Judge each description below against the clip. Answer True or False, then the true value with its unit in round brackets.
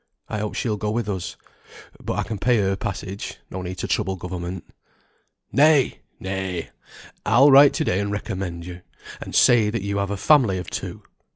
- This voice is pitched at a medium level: False (100 Hz)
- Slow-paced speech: False (185 wpm)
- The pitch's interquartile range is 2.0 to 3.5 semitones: True (3.1 semitones)